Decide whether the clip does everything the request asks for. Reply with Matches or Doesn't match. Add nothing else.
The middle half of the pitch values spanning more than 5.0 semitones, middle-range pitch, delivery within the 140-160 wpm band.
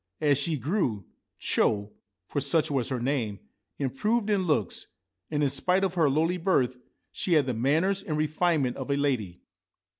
Doesn't match